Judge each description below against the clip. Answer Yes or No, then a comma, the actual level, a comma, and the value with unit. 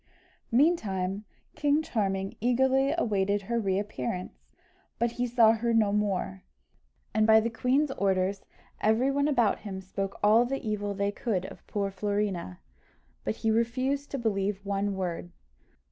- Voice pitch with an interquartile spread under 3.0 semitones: No, average, 3.5 semitones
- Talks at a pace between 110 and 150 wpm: Yes, average, 145 wpm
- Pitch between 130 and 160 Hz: No, high, 210 Hz